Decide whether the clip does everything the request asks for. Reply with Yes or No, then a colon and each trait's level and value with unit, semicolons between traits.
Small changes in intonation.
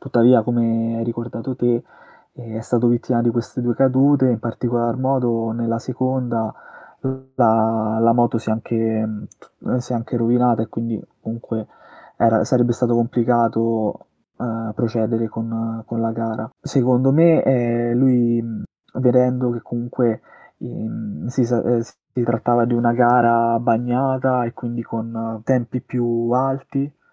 Yes: narrow, 1.6 semitones